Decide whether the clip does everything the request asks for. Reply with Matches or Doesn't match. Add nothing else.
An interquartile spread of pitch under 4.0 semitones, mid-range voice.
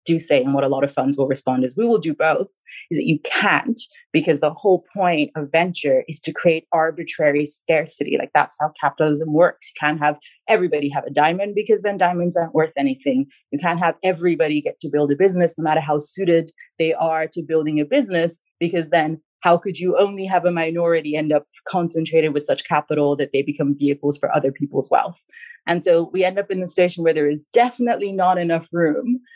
Matches